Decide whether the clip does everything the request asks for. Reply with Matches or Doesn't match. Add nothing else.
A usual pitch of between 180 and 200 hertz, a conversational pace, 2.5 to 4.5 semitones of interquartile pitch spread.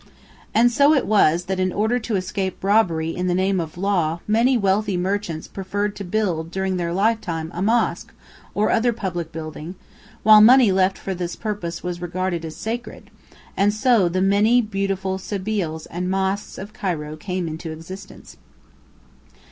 Matches